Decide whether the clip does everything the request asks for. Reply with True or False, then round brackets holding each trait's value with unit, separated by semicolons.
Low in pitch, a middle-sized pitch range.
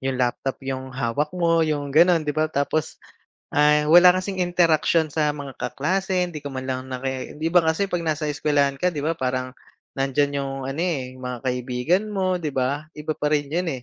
False (150 Hz; 3.6 semitones)